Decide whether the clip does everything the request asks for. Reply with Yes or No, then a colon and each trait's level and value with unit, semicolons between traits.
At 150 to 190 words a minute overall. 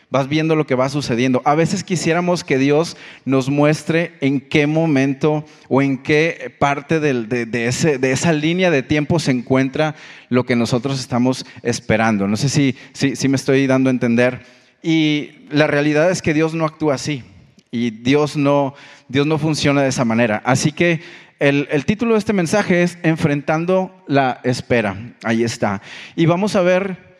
Yes: average, 180 wpm